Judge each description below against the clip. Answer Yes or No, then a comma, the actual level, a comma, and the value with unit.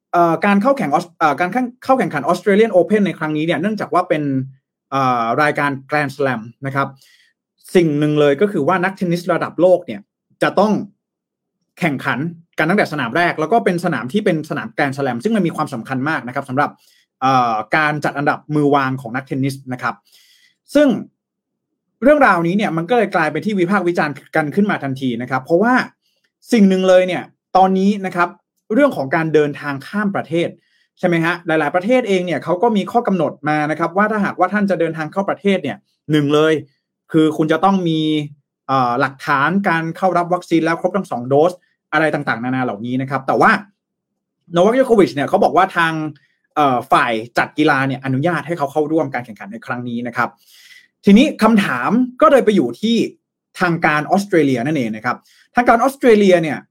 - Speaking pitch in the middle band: Yes, medium, 170 Hz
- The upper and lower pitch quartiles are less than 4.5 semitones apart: No, average, 5.2 semitones